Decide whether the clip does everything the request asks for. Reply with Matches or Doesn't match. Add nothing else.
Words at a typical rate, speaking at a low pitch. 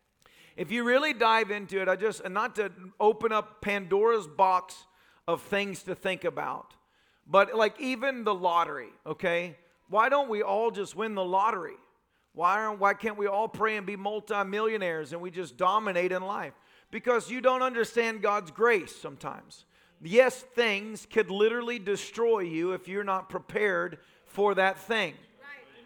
Doesn't match